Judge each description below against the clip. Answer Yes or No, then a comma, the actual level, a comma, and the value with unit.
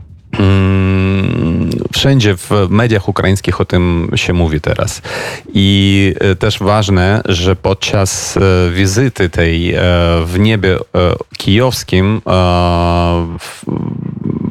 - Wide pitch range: No, average, 2.7 semitones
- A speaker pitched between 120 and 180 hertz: No, very low, 95 Hz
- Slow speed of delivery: Yes, slow, 85 wpm